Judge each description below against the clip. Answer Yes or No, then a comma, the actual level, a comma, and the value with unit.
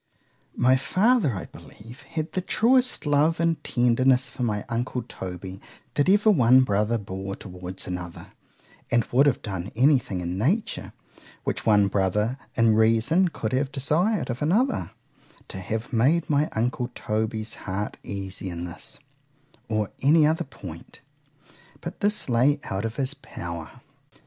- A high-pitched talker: No, low, 120 Hz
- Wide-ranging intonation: Yes, wide, 6.4 semitones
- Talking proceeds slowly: No, average, 150 wpm